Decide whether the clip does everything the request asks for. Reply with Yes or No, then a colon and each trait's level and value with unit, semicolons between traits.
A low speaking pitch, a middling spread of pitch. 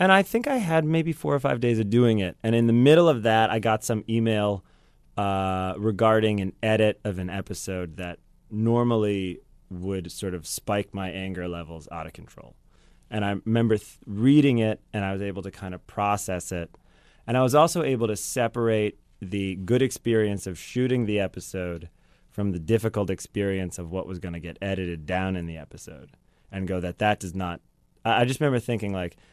Yes: low, 100 Hz; average, 3.7 semitones